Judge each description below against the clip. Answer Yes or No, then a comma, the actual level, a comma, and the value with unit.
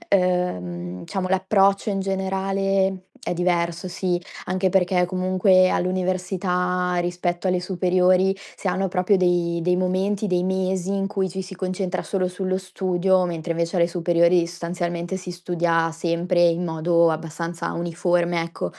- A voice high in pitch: No, medium, 180 Hz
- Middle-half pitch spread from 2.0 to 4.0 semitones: No, narrow, 1.6 semitones